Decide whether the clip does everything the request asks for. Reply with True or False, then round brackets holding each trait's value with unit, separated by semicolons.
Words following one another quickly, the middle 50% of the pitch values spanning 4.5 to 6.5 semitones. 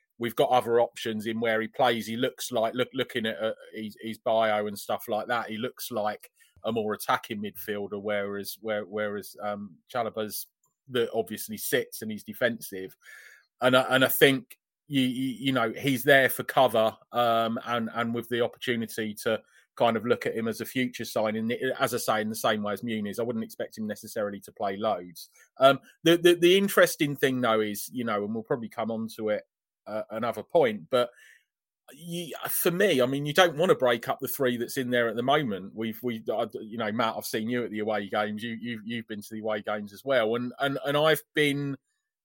False (220 wpm; 3.3 semitones)